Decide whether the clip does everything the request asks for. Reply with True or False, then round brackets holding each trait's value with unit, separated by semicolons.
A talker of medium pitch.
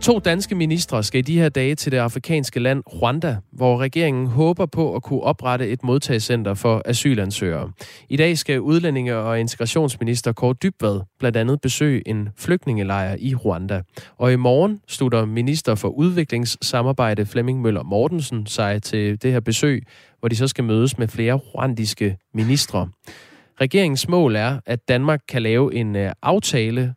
False (125 Hz)